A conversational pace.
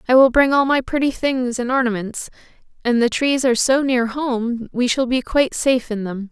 No: fast, 220 wpm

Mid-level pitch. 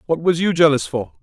Yes: medium, 155 Hz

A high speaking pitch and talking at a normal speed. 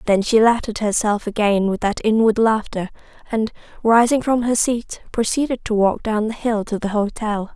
Yes: high, 220 Hz; average, 190 wpm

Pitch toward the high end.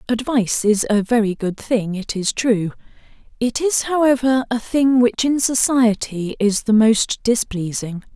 Yes: high, 230 Hz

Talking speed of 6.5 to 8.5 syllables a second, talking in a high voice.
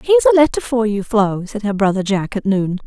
No: 6.0 syllables/s; high, 220 Hz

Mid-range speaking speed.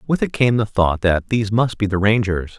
No: fast, 255 wpm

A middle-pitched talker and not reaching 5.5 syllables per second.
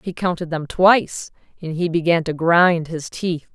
Yes: medium, 170 Hz; 4.4 syllables/s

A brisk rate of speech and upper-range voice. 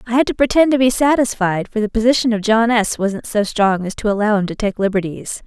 Yes: fast, 250 wpm; high, 220 Hz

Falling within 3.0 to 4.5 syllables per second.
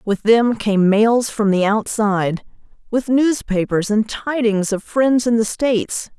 Yes: 4.0 syllables/s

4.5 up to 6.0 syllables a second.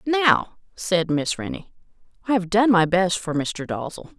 No: 4.3 syllables/s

